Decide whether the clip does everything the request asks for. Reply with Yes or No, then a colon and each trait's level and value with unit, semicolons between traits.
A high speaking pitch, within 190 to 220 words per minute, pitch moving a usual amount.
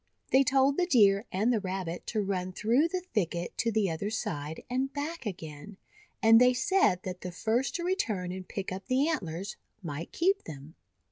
No: high, 210 Hz; average, 195 wpm; wide, 6.5 semitones